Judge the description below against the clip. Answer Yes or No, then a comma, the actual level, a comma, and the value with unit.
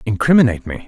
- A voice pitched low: Yes, low, 115 Hz